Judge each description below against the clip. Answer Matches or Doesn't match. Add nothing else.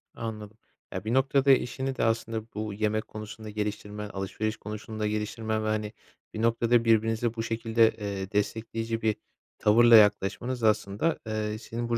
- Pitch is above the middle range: Doesn't match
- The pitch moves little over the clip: Matches